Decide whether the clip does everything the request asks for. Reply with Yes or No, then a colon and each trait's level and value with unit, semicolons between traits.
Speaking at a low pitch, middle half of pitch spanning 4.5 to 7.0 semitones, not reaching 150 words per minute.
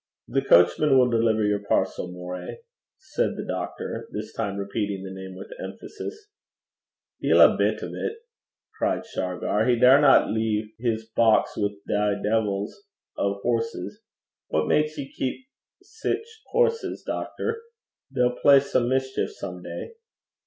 Yes: low, 110 Hz; average, 5.1 semitones; average, 140 wpm